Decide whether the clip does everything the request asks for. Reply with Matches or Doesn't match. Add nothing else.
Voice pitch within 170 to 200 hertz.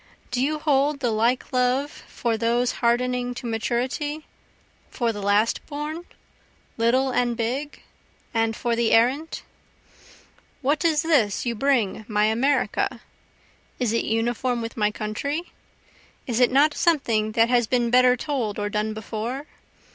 Doesn't match